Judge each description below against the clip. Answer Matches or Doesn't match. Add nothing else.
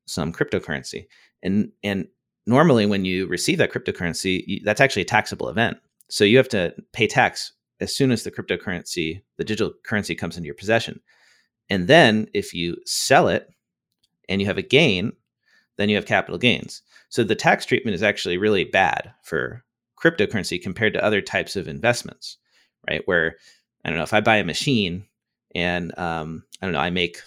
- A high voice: Doesn't match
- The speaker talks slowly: Doesn't match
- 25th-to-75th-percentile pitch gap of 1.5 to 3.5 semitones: Matches